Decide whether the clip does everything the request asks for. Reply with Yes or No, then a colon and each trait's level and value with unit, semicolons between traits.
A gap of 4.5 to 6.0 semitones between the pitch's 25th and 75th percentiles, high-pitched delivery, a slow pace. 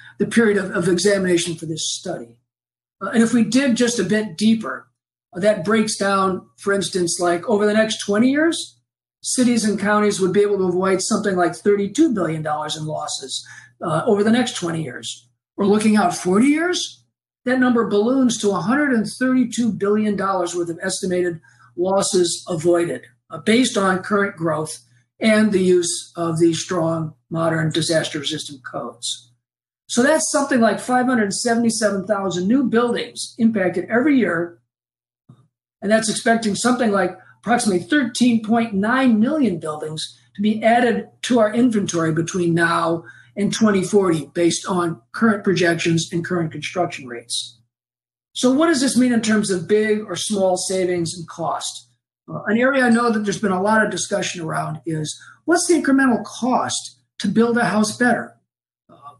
No: average, 5.3 semitones; high, 195 Hz; average, 155 wpm